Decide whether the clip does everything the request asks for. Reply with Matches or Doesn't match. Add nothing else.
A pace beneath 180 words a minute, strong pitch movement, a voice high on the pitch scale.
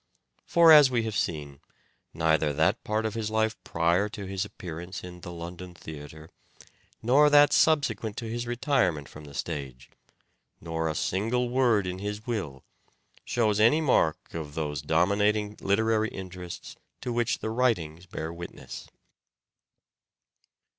Doesn't match